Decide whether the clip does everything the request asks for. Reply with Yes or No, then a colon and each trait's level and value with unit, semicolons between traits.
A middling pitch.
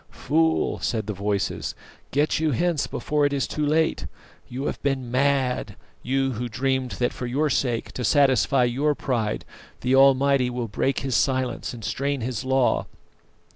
No: low, 130 Hz